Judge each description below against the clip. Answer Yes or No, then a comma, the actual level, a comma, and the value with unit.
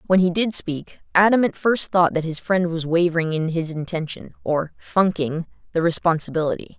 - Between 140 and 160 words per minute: No, average, 175 wpm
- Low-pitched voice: No, medium, 170 Hz